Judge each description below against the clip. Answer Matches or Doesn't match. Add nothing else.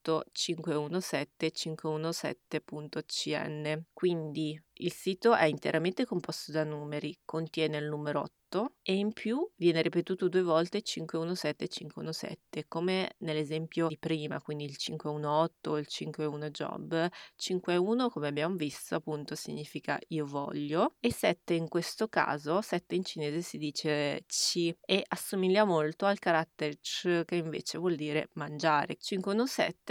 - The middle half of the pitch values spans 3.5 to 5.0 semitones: Doesn't match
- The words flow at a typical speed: Matches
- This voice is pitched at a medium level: Matches